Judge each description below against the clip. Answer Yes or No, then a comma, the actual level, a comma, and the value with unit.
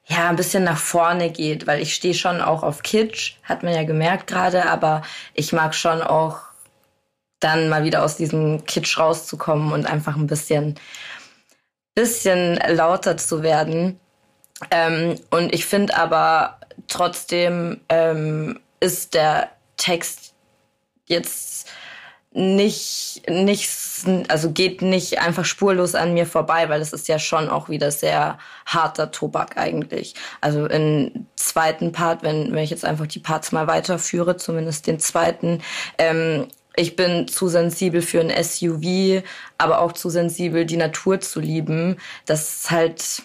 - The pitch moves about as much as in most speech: No, narrow, 2.1 semitones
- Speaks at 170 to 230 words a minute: No, average, 145 wpm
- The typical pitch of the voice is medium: Yes, medium, 165 Hz